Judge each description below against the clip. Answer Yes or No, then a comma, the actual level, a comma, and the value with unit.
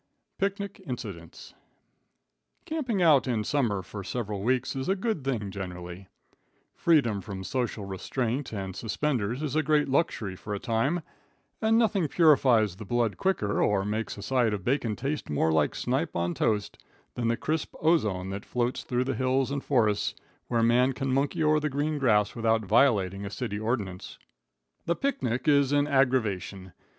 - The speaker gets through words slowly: No, average, 165 wpm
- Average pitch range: No, wide, 5.8 semitones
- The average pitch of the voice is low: Yes, low, 120 Hz